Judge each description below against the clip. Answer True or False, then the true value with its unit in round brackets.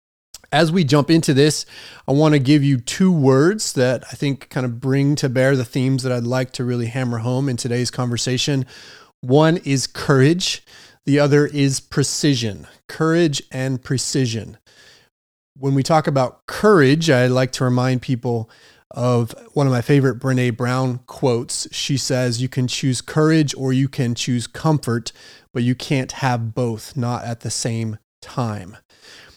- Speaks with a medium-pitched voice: False (130 Hz)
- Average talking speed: True (165 wpm)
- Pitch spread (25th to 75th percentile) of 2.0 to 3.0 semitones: True (2.6 semitones)